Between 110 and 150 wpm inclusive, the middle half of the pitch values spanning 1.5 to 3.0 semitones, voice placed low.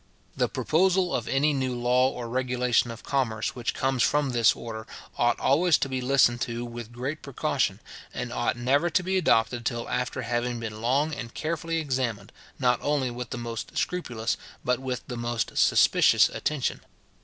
No: average, 175 wpm; average, 2.7 semitones; low, 125 Hz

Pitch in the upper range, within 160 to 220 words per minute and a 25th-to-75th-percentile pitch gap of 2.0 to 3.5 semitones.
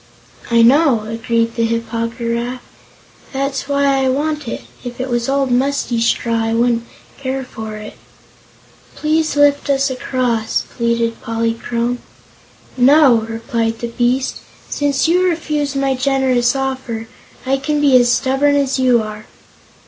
No: very high, 250 Hz; average, 145 wpm; average, 3.0 semitones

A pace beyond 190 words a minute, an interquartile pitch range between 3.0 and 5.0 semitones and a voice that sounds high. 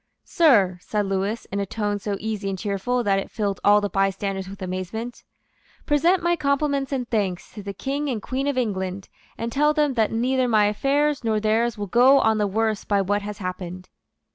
Yes: average, 200 wpm; average, 4.6 semitones; high, 215 Hz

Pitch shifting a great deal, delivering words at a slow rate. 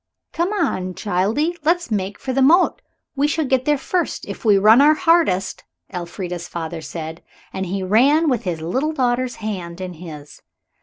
No: wide, 8.6 semitones; average, 170 wpm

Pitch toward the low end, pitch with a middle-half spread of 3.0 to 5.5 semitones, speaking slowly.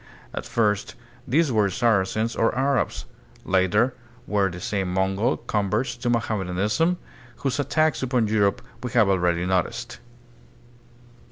Yes: low, 105 Hz; average, 4.5 semitones; slow, 125 wpm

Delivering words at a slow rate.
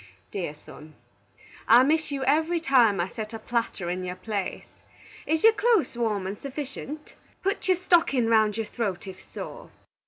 No: average, 165 wpm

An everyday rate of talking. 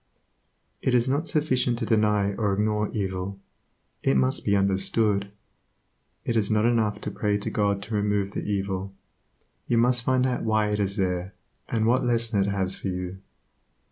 Yes: average, 170 wpm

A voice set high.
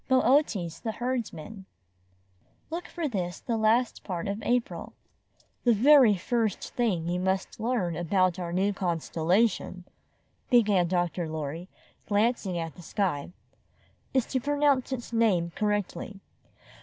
Yes: high, 205 Hz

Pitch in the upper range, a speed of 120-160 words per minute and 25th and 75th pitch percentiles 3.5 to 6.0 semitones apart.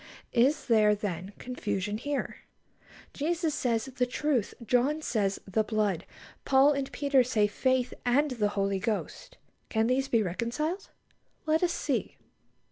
Yes: high, 245 Hz; slow, 135 wpm; average, 4.9 semitones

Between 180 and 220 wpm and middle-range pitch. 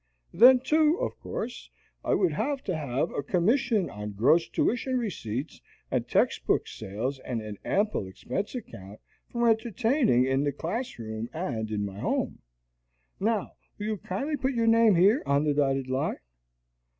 No: average, 160 wpm; medium, 175 Hz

